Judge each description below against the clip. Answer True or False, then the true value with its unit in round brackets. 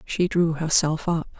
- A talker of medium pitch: True (165 Hz)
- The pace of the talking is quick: False (170 wpm)